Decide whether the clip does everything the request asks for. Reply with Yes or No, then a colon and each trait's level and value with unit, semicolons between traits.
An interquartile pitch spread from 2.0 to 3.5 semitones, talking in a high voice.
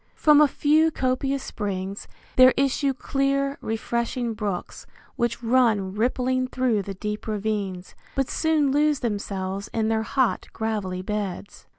No: average, 4.7 semitones; high, 235 Hz